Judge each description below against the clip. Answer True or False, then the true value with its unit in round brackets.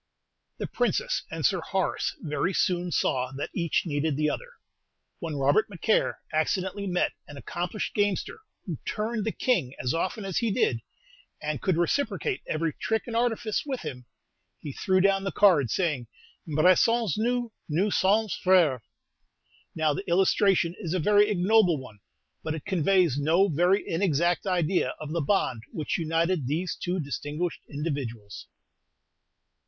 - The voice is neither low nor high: True (175 Hz)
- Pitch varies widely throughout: False (5.0 semitones)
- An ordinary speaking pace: True (150 wpm)